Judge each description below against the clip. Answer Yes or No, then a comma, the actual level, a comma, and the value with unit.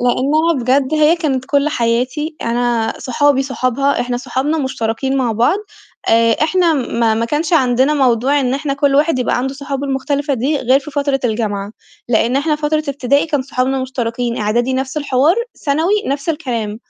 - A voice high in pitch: Yes, very high, 265 Hz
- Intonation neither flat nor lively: Yes, average, 3.1 semitones